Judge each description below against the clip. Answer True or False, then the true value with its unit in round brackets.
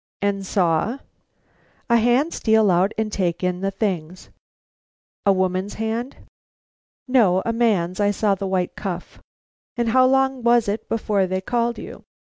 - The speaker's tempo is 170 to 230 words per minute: False (155 wpm)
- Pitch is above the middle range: True (205 Hz)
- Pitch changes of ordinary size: True (4.0 semitones)